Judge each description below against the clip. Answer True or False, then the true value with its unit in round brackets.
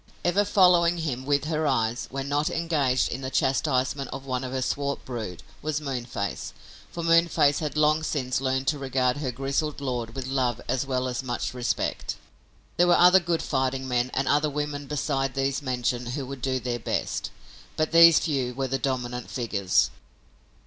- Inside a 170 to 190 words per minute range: True (180 wpm)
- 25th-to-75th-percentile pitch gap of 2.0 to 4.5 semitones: True (2.8 semitones)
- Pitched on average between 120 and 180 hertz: True (135 Hz)